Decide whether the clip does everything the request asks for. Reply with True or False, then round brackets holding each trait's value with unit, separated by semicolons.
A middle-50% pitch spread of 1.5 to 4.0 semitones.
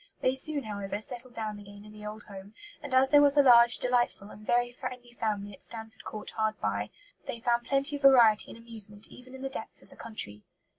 True (3.3 semitones)